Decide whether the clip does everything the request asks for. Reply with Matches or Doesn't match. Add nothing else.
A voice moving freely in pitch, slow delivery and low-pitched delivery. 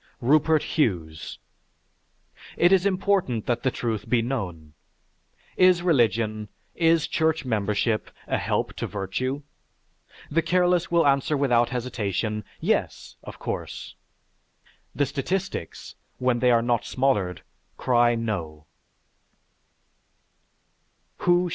Matches